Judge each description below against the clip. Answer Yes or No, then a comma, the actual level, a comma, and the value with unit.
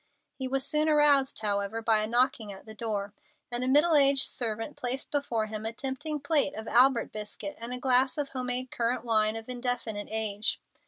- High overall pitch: Yes, high, 245 Hz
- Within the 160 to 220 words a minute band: Yes, average, 200 wpm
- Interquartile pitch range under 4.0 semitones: Yes, average, 3.6 semitones